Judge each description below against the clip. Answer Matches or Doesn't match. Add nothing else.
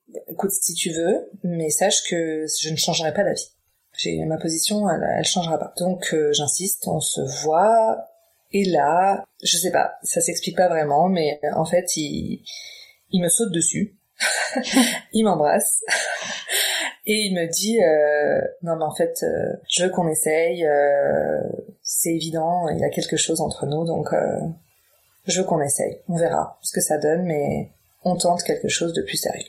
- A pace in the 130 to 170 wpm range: Doesn't match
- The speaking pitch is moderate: Matches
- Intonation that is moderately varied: Matches